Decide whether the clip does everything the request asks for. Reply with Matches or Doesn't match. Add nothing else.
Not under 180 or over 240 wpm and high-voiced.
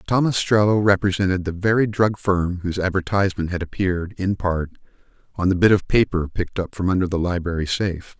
Doesn't match